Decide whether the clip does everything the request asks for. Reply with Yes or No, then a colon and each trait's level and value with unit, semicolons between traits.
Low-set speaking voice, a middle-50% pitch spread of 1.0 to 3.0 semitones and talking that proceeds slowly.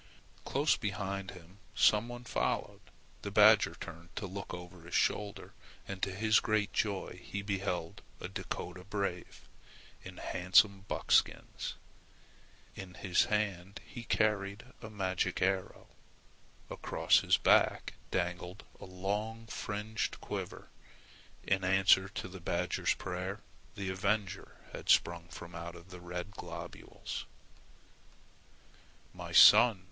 Yes: very low, 95 Hz; narrow, 2.4 semitones; slow, 120 wpm